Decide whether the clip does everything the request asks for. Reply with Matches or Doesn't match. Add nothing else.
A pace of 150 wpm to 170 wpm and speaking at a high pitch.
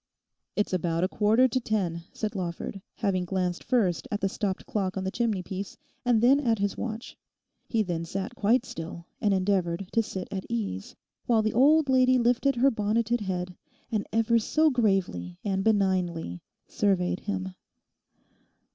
Matches